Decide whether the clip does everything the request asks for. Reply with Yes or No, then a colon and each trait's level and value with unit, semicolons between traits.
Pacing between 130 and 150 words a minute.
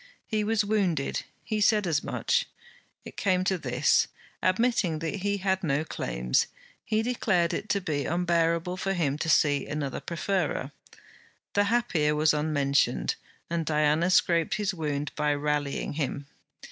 Yes: average, 145 wpm